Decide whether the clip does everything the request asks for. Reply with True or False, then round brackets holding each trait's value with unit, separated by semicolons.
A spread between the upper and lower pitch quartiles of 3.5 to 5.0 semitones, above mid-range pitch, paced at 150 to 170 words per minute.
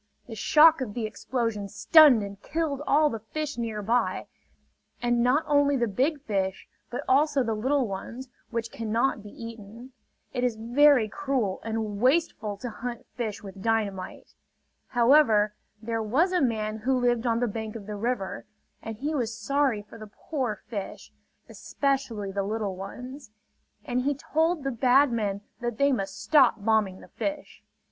True (4.2 semitones; 235 Hz; 165 wpm)